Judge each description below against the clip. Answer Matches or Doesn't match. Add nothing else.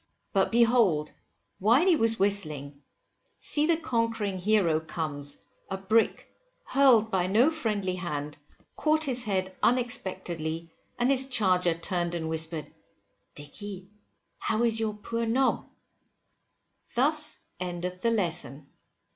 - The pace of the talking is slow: Matches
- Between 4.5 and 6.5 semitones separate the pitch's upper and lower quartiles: Matches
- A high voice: Matches